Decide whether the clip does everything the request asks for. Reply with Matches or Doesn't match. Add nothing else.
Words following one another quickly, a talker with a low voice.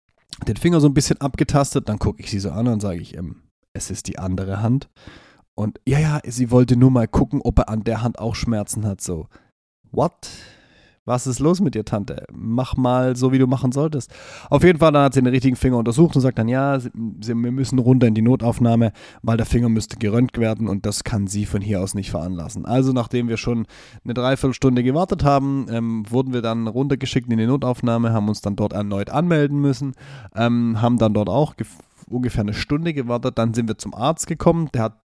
Matches